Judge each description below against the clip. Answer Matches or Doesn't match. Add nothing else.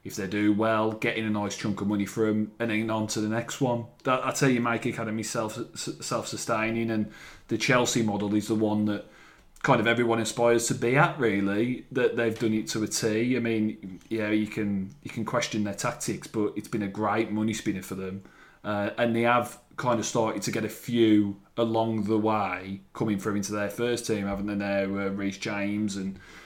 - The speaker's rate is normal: Doesn't match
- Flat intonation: Matches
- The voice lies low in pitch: Matches